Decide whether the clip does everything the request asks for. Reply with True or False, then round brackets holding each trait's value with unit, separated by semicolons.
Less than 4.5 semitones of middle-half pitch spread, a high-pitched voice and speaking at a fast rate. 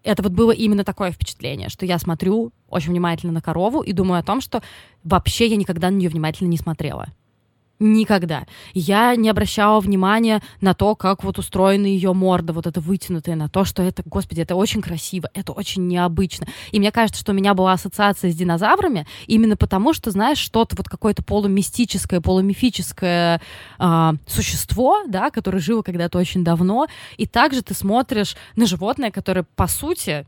True (3.3 semitones; 195 Hz; 175 wpm)